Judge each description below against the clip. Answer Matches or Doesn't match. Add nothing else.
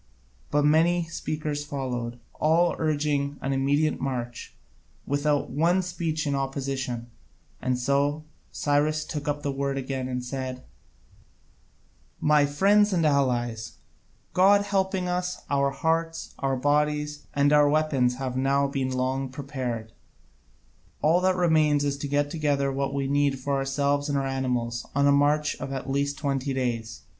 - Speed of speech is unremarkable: Matches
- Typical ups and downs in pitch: Doesn't match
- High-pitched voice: Doesn't match